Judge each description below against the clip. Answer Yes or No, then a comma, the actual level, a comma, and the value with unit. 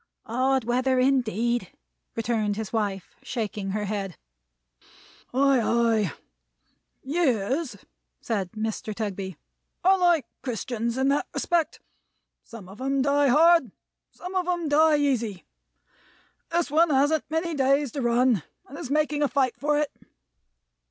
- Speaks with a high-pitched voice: Yes, very high, 260 Hz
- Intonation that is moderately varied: Yes, average, 4.8 semitones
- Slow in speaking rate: Yes, slow, 130 wpm